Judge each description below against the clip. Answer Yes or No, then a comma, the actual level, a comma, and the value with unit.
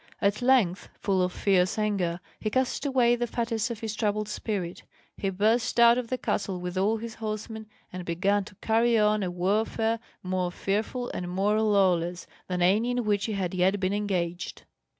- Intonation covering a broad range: No, average, 3.5 semitones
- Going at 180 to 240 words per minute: Yes, average, 185 wpm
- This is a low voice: No, high, 205 Hz